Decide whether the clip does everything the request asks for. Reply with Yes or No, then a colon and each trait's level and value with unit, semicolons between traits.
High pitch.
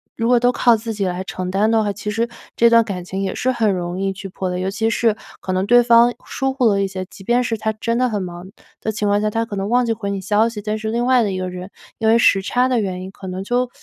Yes: high, 210 Hz